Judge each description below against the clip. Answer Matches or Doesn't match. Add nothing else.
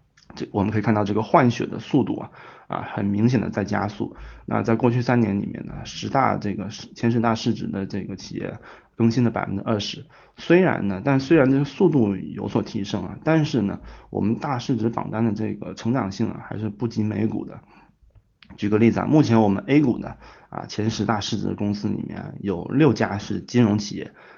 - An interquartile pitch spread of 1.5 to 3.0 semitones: Matches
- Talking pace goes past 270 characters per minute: Matches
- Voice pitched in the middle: Doesn't match